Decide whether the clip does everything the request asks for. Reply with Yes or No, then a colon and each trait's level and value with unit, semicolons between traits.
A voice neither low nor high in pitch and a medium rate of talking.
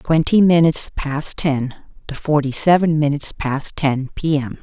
Yes: medium, 150 Hz; average, 155 wpm